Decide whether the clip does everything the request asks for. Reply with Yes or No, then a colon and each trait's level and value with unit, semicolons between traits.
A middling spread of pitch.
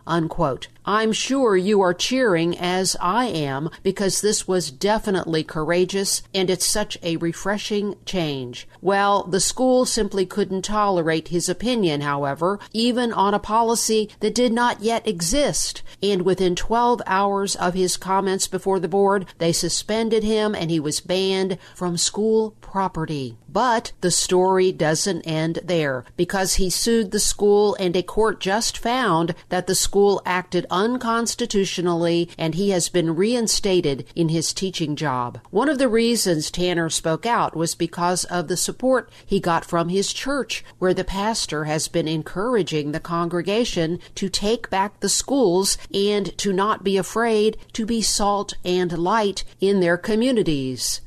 Yes: average, 3.8 semitones